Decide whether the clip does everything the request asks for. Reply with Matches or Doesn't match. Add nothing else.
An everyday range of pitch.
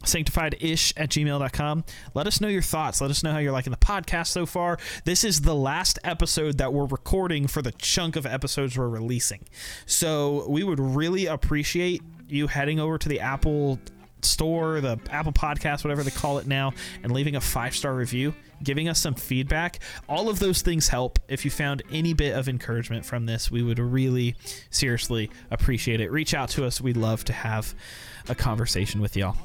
Matches